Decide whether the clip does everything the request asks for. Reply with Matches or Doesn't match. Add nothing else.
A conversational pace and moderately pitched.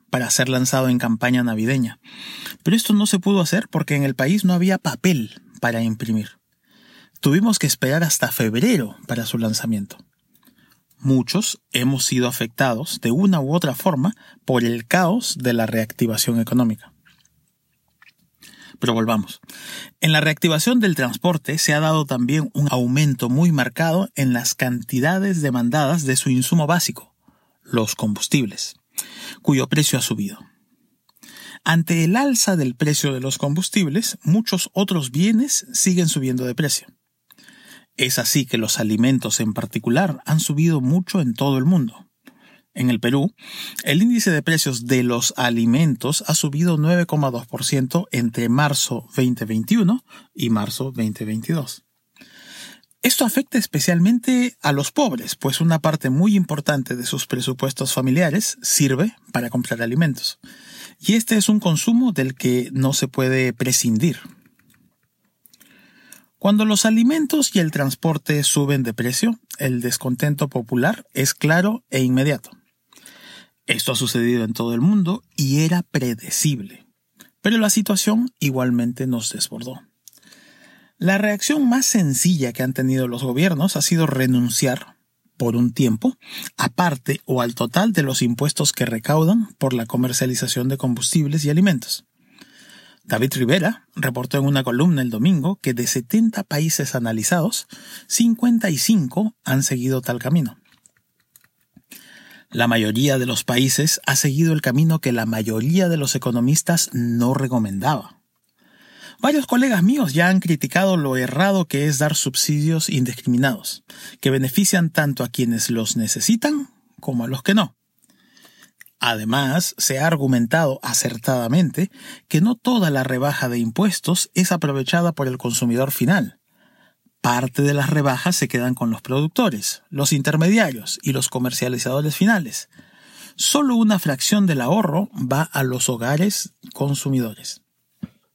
Matches